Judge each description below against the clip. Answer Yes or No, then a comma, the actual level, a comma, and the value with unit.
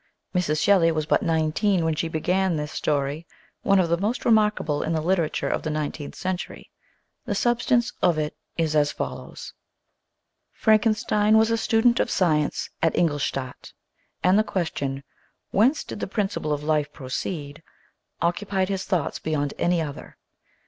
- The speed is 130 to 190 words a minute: Yes, average, 160 wpm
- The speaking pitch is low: No, medium, 170 Hz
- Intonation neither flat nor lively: Yes, average, 4.7 semitones